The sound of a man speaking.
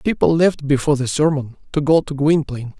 Yes: male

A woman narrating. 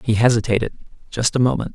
No: male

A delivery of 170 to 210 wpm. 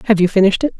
No: fast, 300 wpm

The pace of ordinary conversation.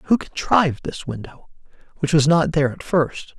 Yes: average, 175 wpm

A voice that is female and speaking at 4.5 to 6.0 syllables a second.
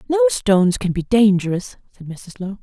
Yes: female; 5.0 syllables/s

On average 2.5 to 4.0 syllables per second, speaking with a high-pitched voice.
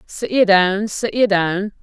Yes: 3.7 syllables/s; high, 205 Hz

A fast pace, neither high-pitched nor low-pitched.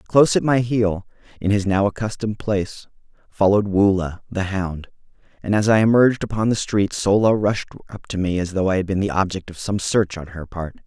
No: fast, 210 wpm; low, 100 Hz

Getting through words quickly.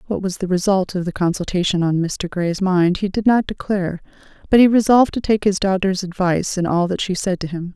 Yes: fast, 230 wpm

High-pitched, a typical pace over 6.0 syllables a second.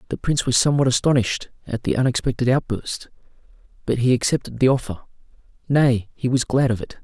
No: low, 125 Hz; 6.4 syllables/s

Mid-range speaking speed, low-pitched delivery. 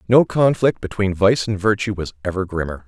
Yes: average, 190 wpm; low, 100 Hz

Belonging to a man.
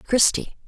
No: female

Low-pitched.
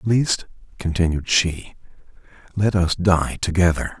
Yes: very low, 90 Hz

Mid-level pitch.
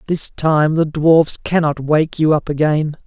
Yes: medium, 155 Hz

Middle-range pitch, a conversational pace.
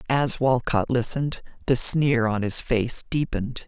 No: low, 125 Hz; average, 145 wpm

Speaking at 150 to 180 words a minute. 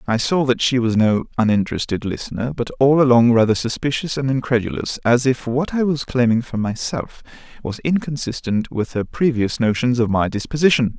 Yes: average, 175 wpm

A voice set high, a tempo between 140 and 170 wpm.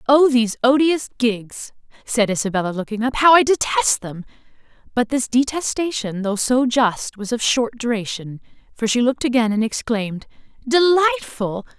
Yes: high, 245 Hz; average, 150 wpm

